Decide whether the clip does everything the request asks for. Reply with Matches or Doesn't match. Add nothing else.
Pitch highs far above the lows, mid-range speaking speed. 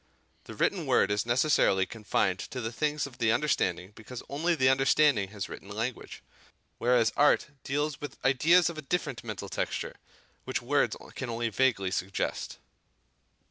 Matches